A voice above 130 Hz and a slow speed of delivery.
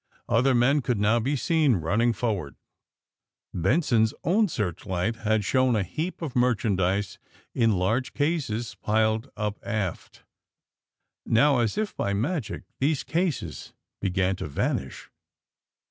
No: low, 115 Hz; slow, 125 wpm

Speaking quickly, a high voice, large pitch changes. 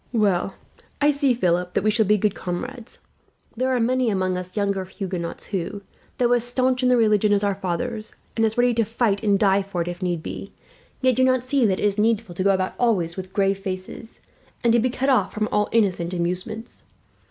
No: fast, 220 wpm; high, 210 Hz; average, 4.2 semitones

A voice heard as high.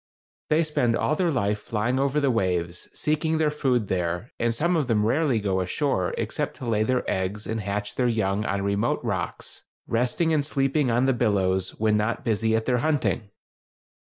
No: low, 115 Hz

